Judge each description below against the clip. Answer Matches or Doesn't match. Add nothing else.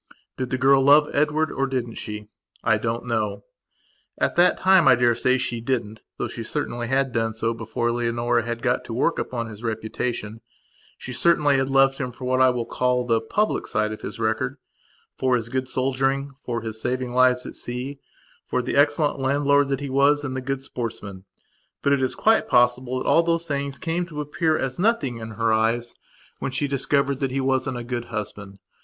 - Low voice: Matches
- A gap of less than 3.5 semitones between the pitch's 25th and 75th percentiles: Matches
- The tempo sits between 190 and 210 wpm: Matches